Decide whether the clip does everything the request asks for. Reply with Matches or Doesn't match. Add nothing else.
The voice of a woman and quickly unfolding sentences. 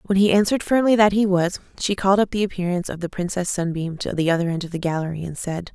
Matches